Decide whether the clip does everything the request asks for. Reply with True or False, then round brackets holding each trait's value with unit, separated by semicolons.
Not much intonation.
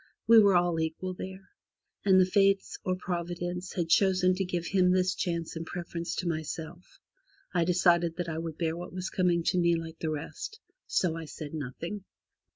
True (1.9 semitones)